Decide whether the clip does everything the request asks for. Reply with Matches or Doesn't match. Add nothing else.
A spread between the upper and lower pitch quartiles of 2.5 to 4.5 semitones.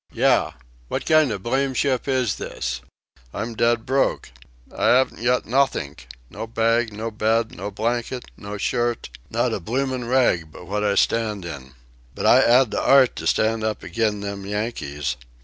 Matches